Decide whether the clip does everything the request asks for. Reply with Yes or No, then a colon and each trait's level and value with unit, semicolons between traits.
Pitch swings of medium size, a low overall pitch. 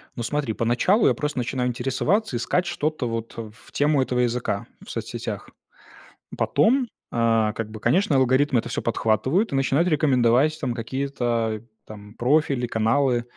Yes: average, 4.1 semitones; low, 125 Hz